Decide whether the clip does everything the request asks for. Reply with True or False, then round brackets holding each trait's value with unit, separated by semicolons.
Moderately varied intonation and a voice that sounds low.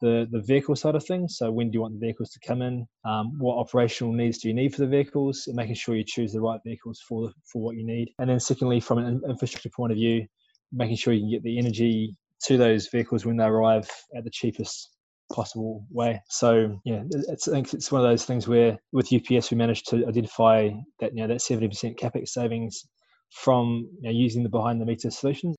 False (1.5 semitones; 115 Hz)